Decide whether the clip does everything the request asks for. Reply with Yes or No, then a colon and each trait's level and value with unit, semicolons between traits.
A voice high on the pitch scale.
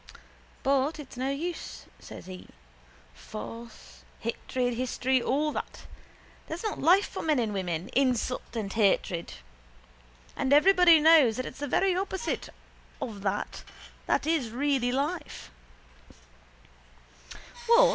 Yes: very high, 260 Hz